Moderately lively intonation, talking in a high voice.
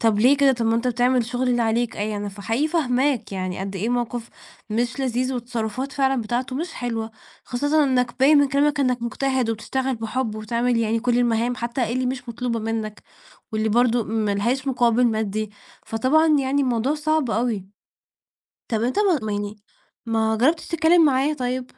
Yes: average, 3.0 semitones; high, 245 Hz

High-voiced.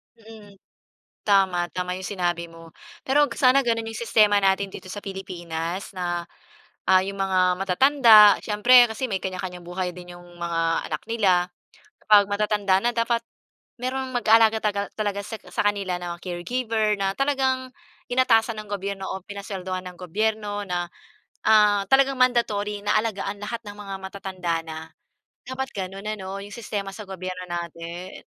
Yes: high, 200 Hz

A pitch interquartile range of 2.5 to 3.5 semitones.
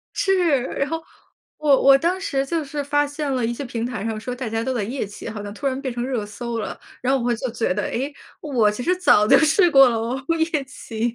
No: average, 4.0 semitones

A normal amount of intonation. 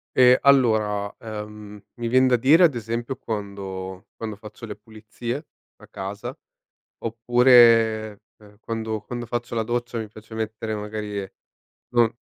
No: narrow, 2.3 semitones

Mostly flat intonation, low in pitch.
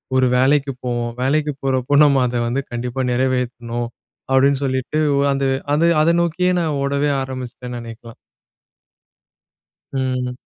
Yes: narrow, 2.3 semitones; low, 130 Hz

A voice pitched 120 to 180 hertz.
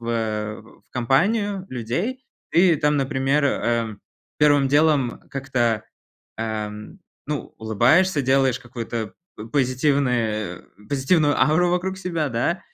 Yes: low, 135 Hz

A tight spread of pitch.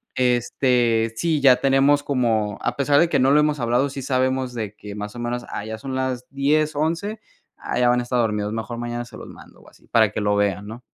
No: average, 3.5 semitones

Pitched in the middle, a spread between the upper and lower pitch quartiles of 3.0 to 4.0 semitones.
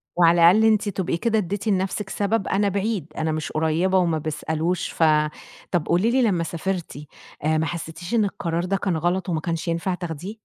Yes: medium, 180 Hz; average, 3.4 semitones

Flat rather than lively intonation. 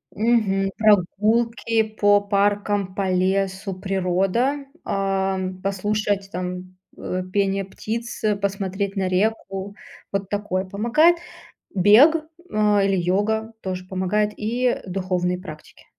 Yes: narrow, 2.2 semitones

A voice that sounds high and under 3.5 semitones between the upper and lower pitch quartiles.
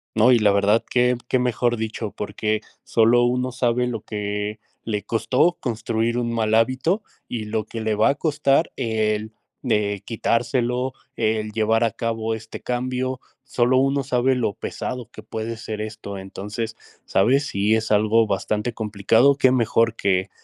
No: low, 115 Hz; narrow, 2.5 semitones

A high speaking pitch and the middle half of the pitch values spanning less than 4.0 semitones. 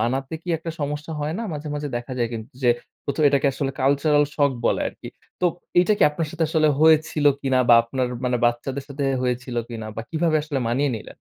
No: medium, 140 Hz; average, 3.6 semitones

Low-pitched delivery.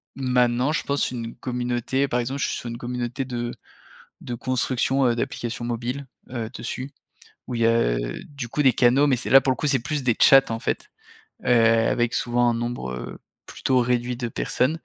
Yes: low, 125 Hz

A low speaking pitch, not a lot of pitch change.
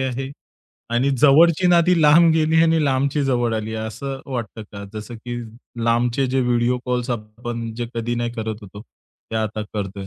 No: low, 120 Hz; average, 3.7 semitones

